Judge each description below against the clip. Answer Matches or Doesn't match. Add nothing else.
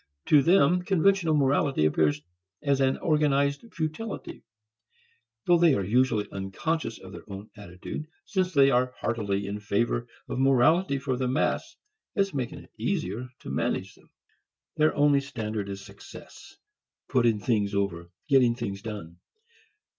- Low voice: Matches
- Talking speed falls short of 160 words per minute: Matches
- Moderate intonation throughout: Doesn't match